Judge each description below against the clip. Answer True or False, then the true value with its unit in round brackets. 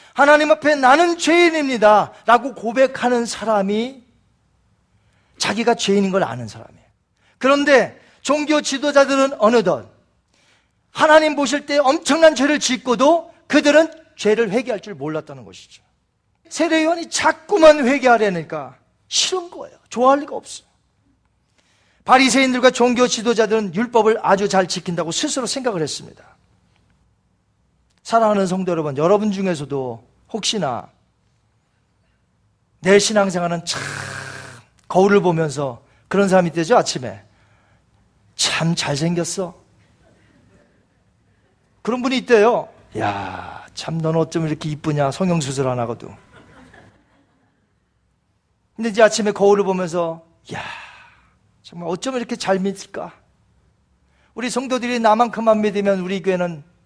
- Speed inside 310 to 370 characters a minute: False (270 characters per minute)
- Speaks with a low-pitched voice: False (210 Hz)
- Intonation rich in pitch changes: True (7.7 semitones)